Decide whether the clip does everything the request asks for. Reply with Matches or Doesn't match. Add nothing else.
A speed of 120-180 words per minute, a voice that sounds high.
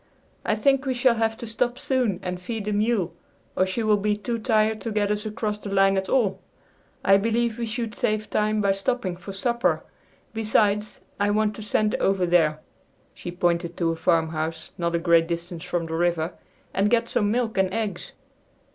Doesn't match